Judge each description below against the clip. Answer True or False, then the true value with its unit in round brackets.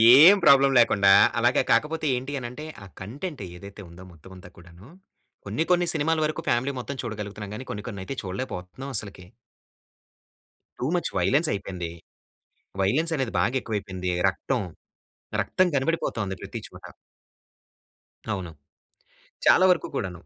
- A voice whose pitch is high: False (115 Hz)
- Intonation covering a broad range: True (6.6 semitones)